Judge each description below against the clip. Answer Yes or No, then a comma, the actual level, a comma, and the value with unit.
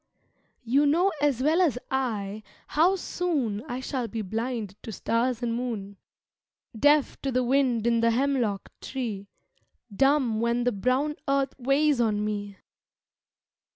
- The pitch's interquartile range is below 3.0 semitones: No, average, 3.8 semitones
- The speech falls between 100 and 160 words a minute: Yes, average, 140 wpm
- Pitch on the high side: Yes, high, 245 Hz